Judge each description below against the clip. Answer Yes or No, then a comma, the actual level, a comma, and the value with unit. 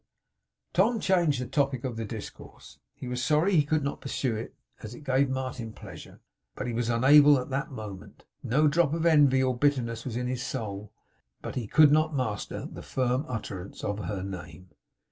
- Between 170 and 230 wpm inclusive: Yes, average, 185 wpm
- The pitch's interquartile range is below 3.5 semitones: No, average, 4.0 semitones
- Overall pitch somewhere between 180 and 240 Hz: No, low, 130 Hz